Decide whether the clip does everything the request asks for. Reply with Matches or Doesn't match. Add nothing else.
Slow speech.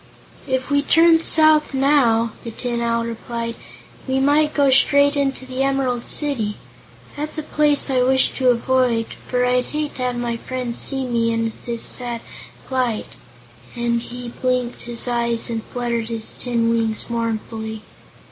Doesn't match